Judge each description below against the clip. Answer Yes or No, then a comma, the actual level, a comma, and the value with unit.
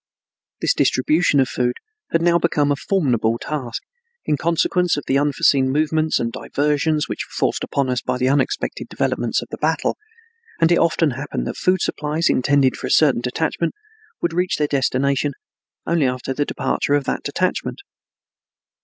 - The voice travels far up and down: No, average, 3.6 semitones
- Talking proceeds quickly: No, average, 170 wpm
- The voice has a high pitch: No, medium, 145 Hz